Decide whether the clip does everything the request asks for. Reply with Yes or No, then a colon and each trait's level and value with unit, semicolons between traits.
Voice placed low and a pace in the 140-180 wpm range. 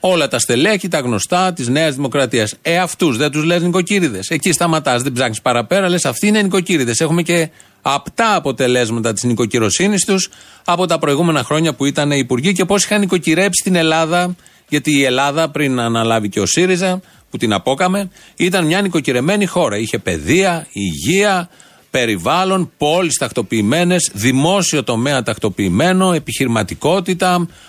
No: medium, 160 Hz; average, 150 wpm